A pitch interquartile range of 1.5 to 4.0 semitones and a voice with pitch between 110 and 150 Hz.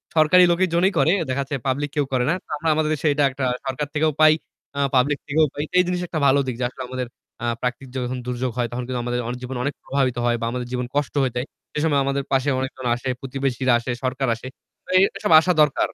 Yes: average, 2.8 semitones; low, 135 Hz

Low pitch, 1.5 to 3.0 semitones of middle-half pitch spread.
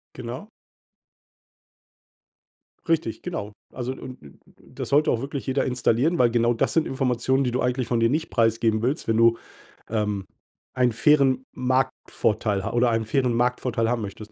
Yes: low, 125 Hz; narrow, 2.5 semitones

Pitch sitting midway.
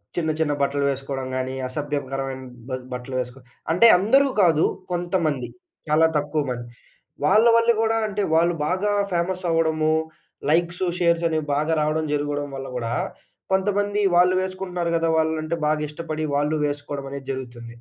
Yes: medium, 155 Hz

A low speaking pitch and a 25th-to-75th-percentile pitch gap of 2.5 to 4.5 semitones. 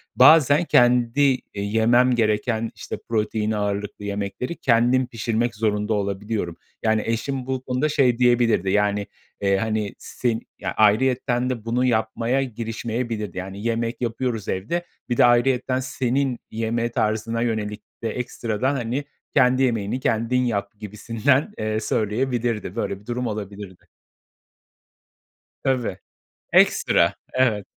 Yes: low, 115 Hz; average, 2.9 semitones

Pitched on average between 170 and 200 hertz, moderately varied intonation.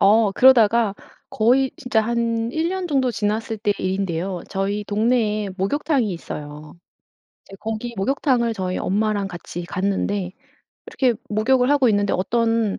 No: high, 215 Hz; average, 3.5 semitones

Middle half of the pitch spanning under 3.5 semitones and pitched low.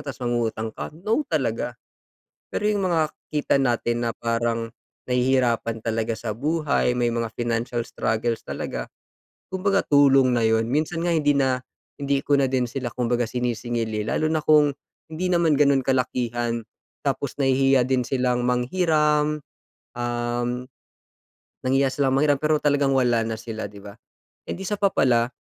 No: average, 3.8 semitones; low, 125 Hz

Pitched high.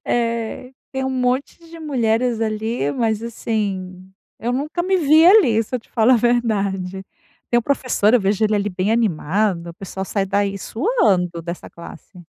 Yes: high, 220 Hz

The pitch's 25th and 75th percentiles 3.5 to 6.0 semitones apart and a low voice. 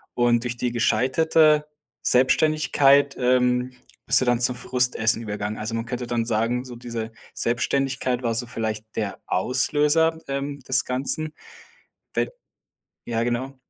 No: average, 2.7 semitones; low, 125 Hz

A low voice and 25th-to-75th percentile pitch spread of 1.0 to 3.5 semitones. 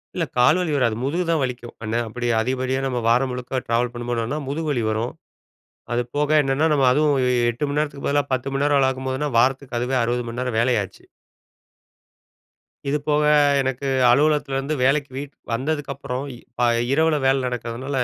Yes: low, 130 Hz; average, 2.9 semitones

